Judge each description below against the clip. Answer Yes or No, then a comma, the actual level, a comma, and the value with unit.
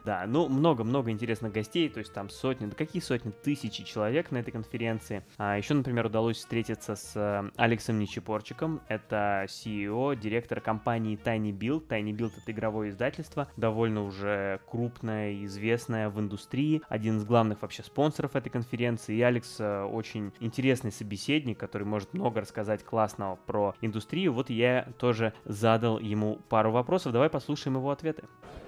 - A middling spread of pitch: Yes, average, 3.0 semitones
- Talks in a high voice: No, low, 115 Hz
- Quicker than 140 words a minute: Yes, average, 150 wpm